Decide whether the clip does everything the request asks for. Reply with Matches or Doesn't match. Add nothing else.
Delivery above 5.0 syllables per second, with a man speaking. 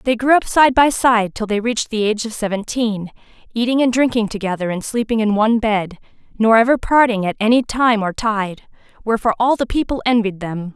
Doesn't match